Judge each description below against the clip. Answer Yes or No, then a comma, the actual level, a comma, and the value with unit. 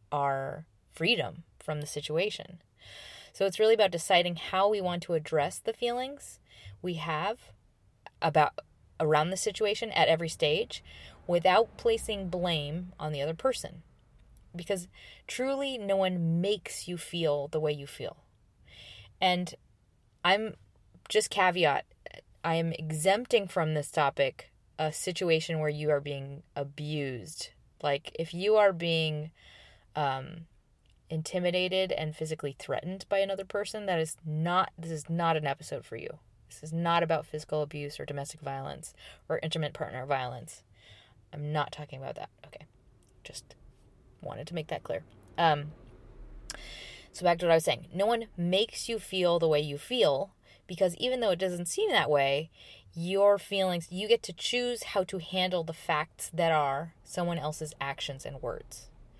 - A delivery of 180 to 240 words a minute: No, average, 155 wpm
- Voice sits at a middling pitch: Yes, medium, 165 Hz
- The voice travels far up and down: No, average, 4.6 semitones